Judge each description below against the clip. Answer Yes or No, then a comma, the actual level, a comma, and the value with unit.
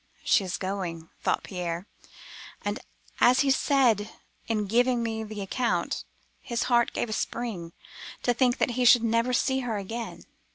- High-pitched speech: Yes, high, 230 Hz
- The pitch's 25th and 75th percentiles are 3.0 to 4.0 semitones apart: Yes, average, 3.5 semitones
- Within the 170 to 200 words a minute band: No, average, 160 wpm